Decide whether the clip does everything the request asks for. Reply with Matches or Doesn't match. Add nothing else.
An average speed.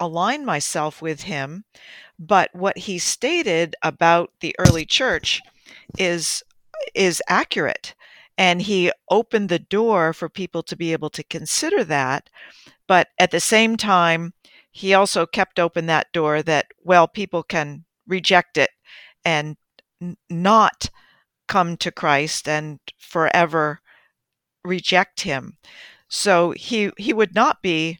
Doesn't match